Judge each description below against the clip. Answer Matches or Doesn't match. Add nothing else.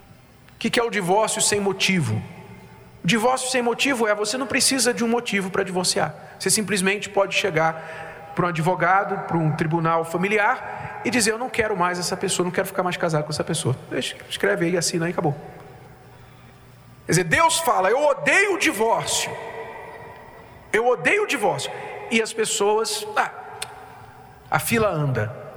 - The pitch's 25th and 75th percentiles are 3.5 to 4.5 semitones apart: Doesn't match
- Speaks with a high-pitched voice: Matches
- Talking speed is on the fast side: Doesn't match